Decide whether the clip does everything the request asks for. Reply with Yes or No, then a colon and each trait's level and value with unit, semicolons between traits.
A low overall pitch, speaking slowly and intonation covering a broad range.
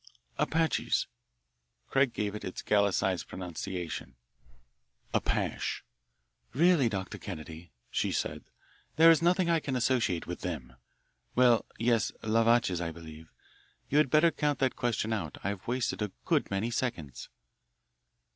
Yes: low, 110 Hz; slow, 130 wpm; wide, 6.5 semitones